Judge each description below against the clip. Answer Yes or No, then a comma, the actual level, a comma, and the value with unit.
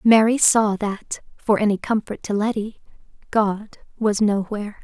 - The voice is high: Yes, high, 210 Hz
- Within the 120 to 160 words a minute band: Yes, slow, 135 wpm